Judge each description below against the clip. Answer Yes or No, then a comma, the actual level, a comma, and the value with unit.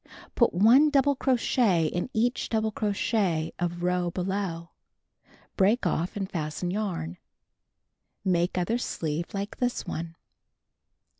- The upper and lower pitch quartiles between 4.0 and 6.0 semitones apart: Yes, average, 4.5 semitones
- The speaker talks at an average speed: No, slow, 120 wpm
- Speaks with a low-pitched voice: No, high, 190 Hz